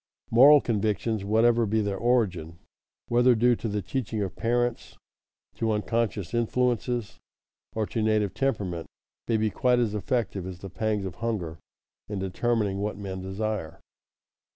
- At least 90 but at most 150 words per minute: Yes, average, 145 wpm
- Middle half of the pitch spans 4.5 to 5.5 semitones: No, average, 3.3 semitones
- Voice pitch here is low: Yes, low, 110 Hz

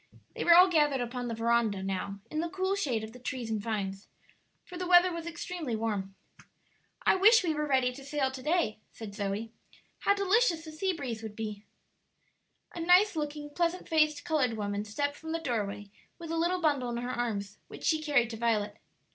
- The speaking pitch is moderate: No, very high, 265 Hz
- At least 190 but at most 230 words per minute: Yes, average, 200 wpm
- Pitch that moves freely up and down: Yes, wide, 7.0 semitones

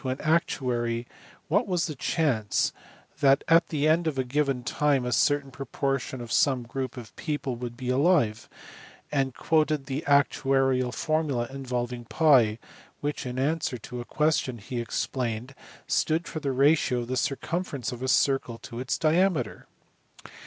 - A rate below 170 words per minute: Yes, average, 155 wpm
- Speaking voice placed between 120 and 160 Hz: Yes, low, 135 Hz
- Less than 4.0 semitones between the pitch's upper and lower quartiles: Yes, average, 3.5 semitones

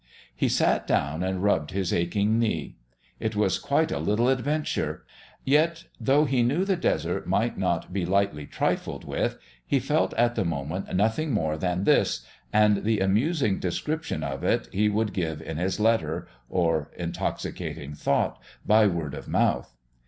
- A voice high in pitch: No, low, 100 Hz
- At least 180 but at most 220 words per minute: No, average, 160 wpm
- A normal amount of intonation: No, wide, 6.2 semitones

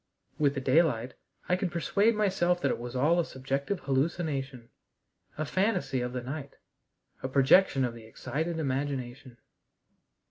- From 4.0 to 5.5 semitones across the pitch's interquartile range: Yes, average, 4.8 semitones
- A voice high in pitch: No, medium, 140 Hz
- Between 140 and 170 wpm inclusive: Yes, average, 145 wpm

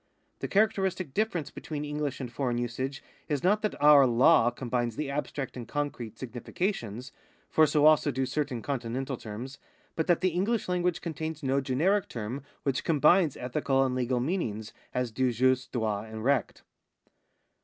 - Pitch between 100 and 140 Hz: Yes, low, 135 Hz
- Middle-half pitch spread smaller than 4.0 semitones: No, average, 4.3 semitones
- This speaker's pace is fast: No, average, 160 wpm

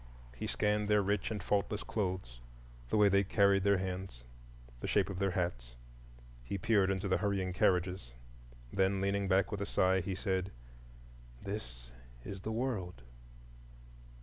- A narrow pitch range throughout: Yes, narrow, 1.8 semitones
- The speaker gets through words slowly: No, average, 150 wpm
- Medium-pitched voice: No, very low, 95 Hz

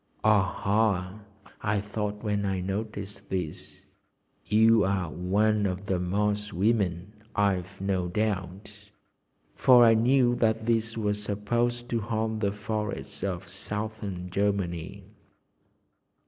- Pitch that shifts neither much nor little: No, narrow, 2.3 semitones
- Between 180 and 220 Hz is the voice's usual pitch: No, low, 105 Hz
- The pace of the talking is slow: Yes, slow, 115 wpm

